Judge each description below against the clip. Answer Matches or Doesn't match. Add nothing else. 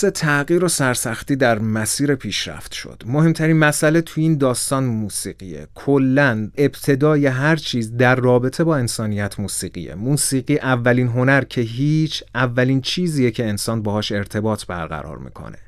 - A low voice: Matches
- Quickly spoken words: Doesn't match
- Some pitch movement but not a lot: Matches